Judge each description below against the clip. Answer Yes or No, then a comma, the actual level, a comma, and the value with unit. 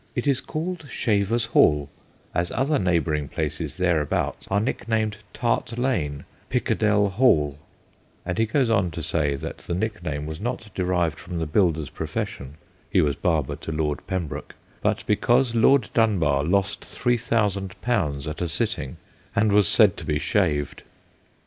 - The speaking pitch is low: Yes, very low, 95 Hz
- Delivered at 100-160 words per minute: Yes, average, 155 wpm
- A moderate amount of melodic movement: No, wide, 6.4 semitones